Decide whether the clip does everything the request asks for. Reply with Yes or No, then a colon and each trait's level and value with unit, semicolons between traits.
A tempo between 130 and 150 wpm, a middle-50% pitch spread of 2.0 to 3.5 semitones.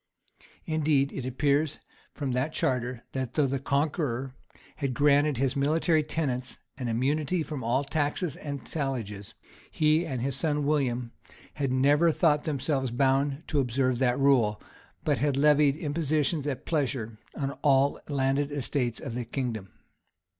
Yes: average, 145 wpm; narrow, 2.6 semitones